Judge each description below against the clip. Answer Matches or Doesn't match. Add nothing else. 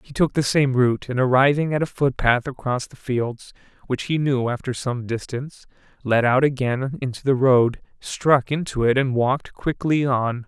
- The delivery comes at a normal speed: Matches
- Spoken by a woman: Doesn't match